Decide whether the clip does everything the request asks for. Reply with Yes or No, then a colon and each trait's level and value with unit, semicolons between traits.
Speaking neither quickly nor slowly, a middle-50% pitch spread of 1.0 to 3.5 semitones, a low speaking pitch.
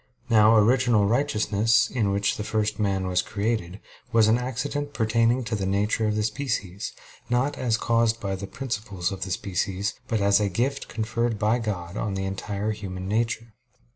Yes: average, 175 wpm; average, 2.7 semitones; low, 110 Hz